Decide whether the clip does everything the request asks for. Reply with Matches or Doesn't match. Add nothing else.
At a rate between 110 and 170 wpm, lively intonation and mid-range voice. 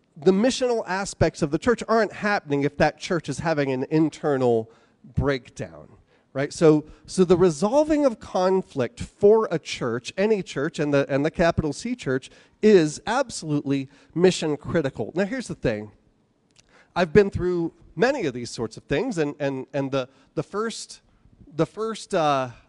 Matches